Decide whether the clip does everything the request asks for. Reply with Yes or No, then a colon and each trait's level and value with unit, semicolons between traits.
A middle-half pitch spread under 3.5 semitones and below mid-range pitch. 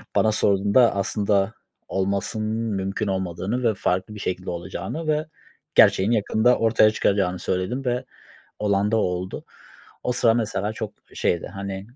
Yes: average, 2.8 semitones; low, 100 Hz